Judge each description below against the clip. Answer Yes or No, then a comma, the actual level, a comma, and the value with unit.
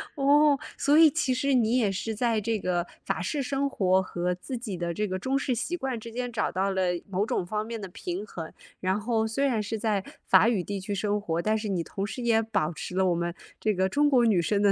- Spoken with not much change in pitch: No, average, 4.6 semitones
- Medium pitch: No, high, 215 Hz